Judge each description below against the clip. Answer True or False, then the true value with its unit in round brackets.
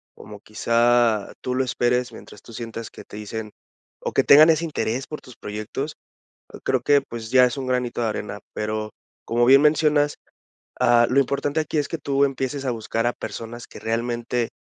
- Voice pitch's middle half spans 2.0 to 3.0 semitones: False (3.4 semitones)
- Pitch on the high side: False (120 Hz)